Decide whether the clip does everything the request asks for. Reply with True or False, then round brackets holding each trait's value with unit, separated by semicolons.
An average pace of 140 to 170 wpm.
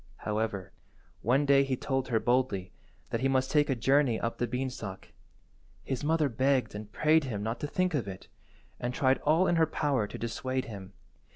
False (190 wpm)